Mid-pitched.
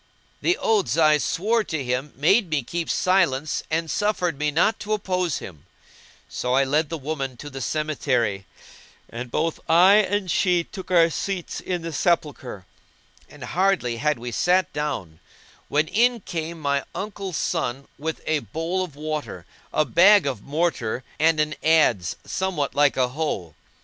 Yes: medium, 155 Hz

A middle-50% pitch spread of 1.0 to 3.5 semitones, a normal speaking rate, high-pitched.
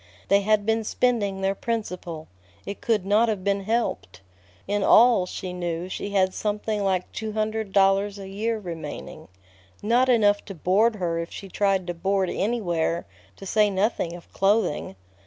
Yes: average, 2.8 semitones; average, 165 wpm; high, 200 Hz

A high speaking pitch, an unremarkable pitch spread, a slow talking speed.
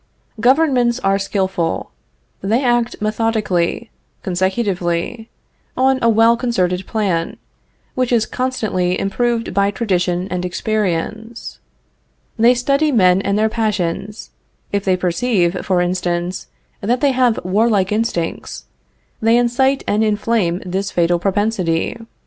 Yes: high, 210 Hz; average, 4.4 semitones; slow, 115 wpm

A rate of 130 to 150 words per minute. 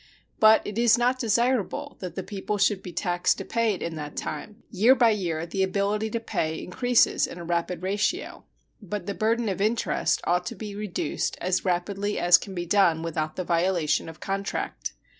No: average, 195 wpm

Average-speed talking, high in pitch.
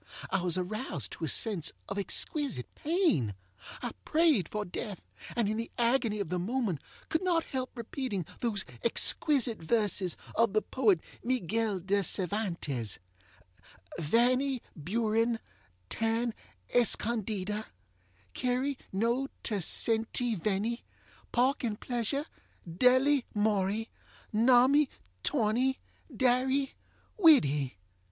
No: slow, 110 wpm; high, 225 Hz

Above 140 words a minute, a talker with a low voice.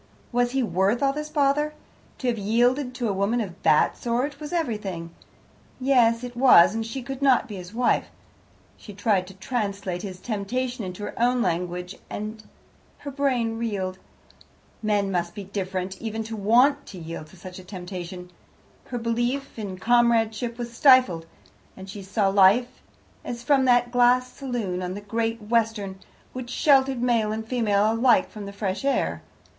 No: average, 170 wpm; high, 225 Hz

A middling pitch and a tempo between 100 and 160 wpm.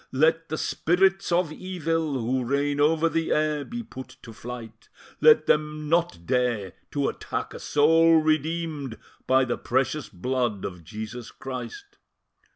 Yes: medium, 150 Hz; average, 145 wpm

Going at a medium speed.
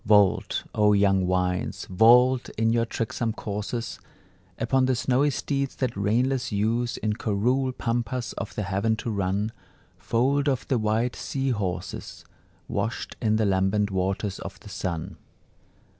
Yes: average, 145 wpm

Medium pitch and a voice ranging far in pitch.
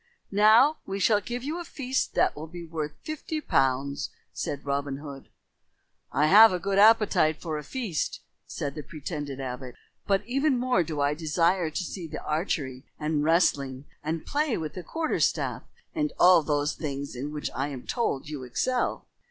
Yes: medium, 160 Hz; wide, 6.8 semitones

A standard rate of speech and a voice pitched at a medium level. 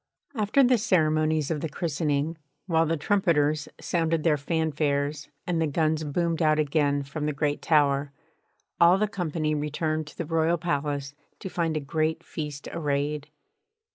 Yes: average, 155 wpm; medium, 155 Hz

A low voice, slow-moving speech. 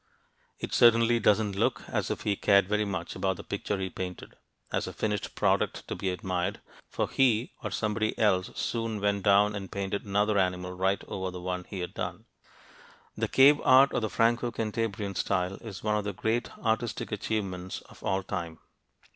No: low, 100 Hz; average, 185 wpm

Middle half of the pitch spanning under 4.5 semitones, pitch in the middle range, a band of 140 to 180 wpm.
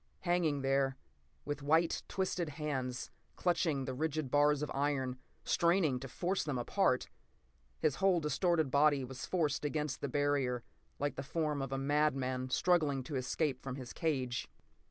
Yes: average, 2.9 semitones; medium, 145 Hz; average, 155 wpm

